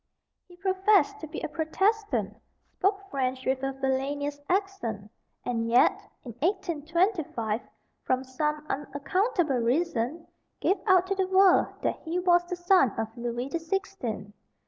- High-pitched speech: Yes, very high, 310 Hz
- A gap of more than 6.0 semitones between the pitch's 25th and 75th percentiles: Yes, wide, 6.6 semitones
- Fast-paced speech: No, average, 140 wpm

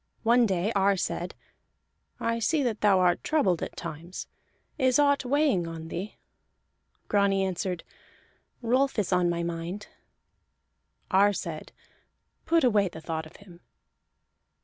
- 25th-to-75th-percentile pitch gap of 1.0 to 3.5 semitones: No, average, 5.1 semitones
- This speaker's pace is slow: Yes, slow, 130 wpm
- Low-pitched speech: No, high, 195 Hz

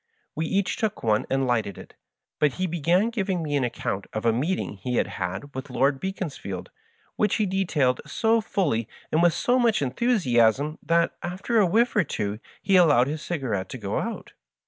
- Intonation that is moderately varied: No, wide, 7.5 semitones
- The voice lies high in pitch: No, medium, 155 Hz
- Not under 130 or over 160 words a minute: No, average, 190 wpm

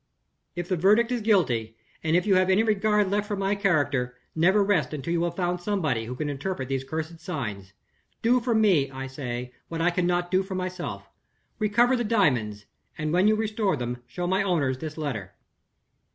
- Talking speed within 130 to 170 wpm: No, average, 195 wpm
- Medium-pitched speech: Yes, medium, 175 Hz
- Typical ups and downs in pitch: No, wide, 6.9 semitones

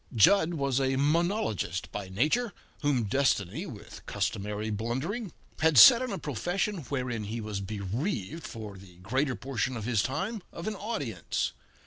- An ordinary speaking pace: Yes, average, 150 wpm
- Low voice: Yes, low, 130 Hz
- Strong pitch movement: Yes, wide, 7.9 semitones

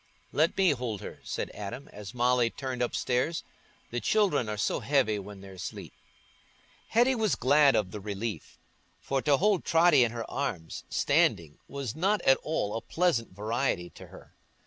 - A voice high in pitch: No, low, 125 Hz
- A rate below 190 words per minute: Yes, average, 170 wpm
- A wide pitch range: Yes, wide, 6.3 semitones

